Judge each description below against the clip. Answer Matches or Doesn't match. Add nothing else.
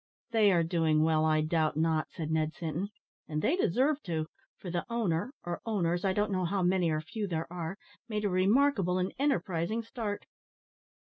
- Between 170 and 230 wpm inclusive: Matches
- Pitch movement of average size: Matches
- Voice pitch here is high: Doesn't match